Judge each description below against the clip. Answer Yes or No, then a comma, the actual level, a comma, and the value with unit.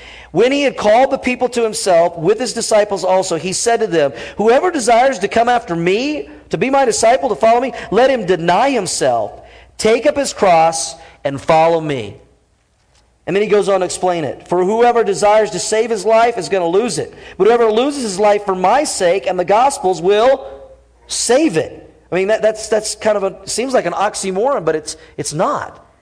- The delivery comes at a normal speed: No, fast, 210 wpm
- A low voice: No, high, 210 Hz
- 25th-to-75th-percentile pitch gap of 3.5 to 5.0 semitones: Yes, average, 4.6 semitones